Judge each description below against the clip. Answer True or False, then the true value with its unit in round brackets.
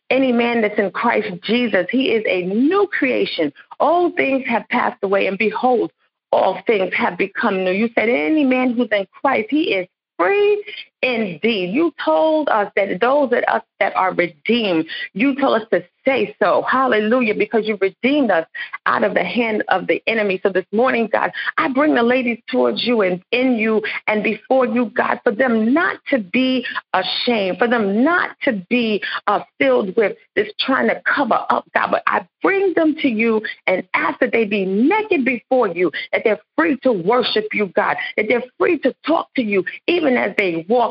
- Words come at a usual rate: True (190 wpm)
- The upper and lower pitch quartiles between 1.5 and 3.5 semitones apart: False (4.8 semitones)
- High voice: True (245 Hz)